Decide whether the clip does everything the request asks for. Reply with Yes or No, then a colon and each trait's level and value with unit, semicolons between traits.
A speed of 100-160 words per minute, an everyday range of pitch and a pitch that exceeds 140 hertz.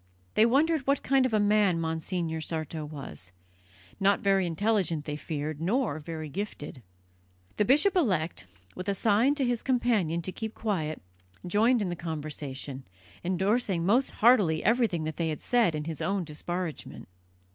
No: average, 155 wpm; wide, 6.1 semitones; medium, 185 Hz